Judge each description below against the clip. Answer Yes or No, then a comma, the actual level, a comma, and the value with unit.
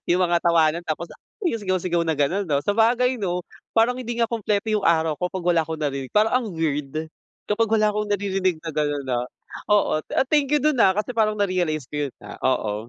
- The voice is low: No, medium, 185 Hz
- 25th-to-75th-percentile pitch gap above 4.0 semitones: Yes, wide, 5.5 semitones